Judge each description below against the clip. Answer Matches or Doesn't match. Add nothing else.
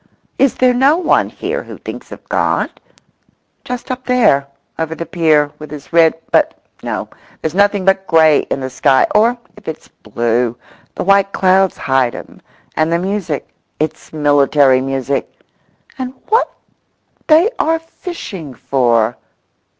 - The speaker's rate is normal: Doesn't match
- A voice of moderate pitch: Matches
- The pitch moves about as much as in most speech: Doesn't match